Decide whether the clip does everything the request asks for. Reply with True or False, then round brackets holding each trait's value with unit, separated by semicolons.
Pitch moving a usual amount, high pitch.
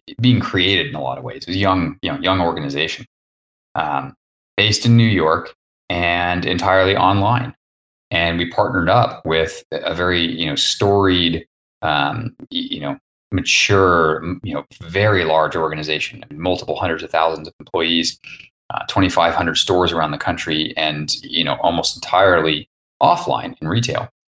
False (3.4 semitones; 85 Hz)